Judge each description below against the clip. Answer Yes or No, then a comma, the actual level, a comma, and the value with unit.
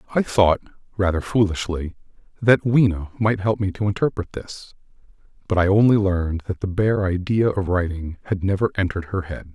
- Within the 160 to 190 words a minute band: Yes, average, 170 wpm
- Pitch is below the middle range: Yes, very low, 95 Hz